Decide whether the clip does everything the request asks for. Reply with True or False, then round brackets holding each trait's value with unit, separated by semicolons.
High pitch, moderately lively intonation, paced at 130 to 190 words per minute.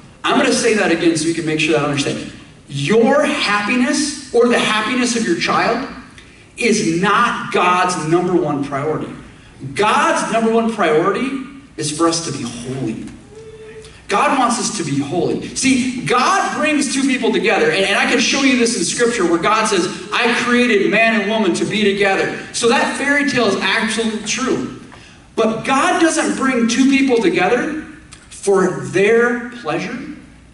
False (225 Hz; 6.4 semitones; 170 wpm)